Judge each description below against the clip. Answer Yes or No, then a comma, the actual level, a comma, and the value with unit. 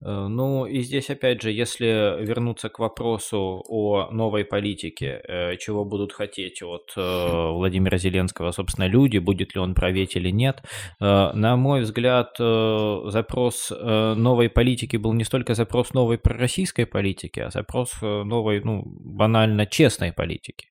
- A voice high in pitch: No, low, 110 Hz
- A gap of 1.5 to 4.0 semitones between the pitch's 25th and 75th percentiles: Yes, average, 3.5 semitones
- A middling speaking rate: Yes, average, 135 wpm